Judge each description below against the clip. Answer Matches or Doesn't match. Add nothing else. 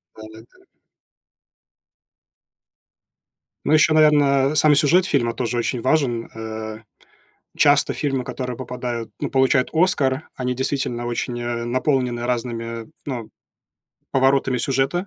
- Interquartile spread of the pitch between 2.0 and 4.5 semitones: Matches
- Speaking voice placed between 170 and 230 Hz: Doesn't match